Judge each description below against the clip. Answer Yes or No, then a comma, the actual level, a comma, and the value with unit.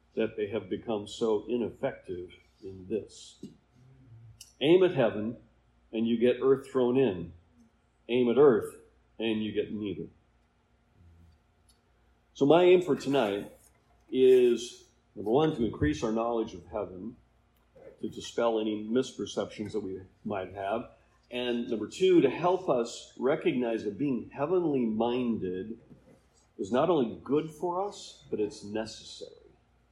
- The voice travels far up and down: Yes, wide, 8.3 semitones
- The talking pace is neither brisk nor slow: No, slow, 130 wpm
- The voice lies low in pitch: Yes, low, 125 Hz